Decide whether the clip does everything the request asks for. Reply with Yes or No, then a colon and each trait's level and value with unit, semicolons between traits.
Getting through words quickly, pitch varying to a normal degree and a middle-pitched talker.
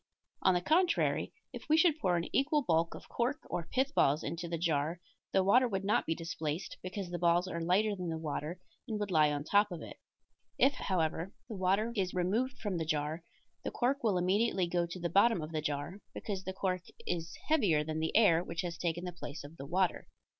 Yes: fast, 220 wpm; average, 3.9 semitones; medium, 180 Hz